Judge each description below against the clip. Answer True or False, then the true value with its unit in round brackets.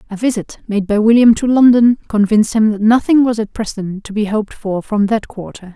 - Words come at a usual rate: False (220 wpm)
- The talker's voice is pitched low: False (215 Hz)